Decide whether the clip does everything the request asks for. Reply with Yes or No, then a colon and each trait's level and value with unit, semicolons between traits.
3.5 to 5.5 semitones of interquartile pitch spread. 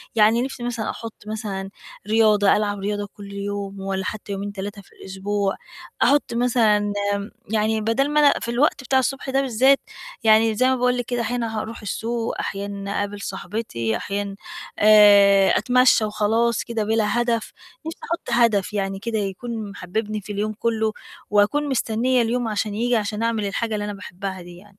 No: narrow, 2.6 semitones